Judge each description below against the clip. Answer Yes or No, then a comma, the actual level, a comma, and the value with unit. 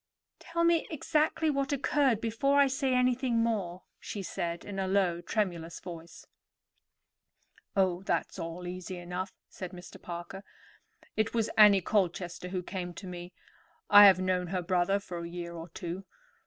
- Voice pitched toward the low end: No, high, 190 Hz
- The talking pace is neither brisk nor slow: Yes, average, 155 wpm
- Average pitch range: Yes, average, 4.4 semitones